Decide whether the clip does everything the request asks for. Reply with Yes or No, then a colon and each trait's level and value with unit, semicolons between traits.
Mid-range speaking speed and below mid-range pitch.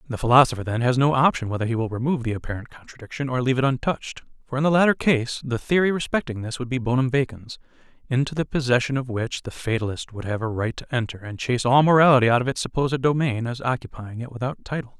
No: fast, 230 wpm; low, 125 Hz